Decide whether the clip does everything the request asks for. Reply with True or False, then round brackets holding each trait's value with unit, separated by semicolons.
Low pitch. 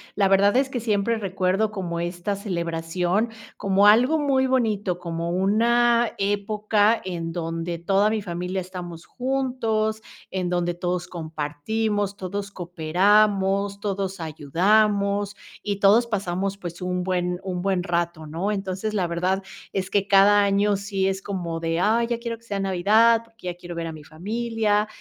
False (195 Hz)